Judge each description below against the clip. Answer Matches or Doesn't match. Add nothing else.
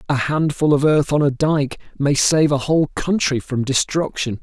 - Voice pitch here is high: Doesn't match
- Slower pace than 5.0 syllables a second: Matches